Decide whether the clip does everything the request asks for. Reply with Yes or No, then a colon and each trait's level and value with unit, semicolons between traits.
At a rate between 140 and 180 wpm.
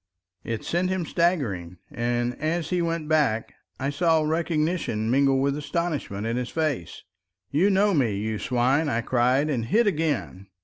Yes: average, 160 wpm